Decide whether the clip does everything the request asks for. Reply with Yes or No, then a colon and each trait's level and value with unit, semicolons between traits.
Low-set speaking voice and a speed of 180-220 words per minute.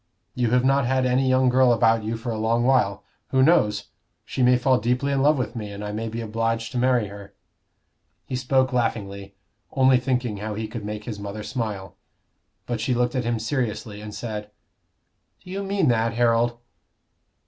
Yes: low, 115 Hz; average, 190 wpm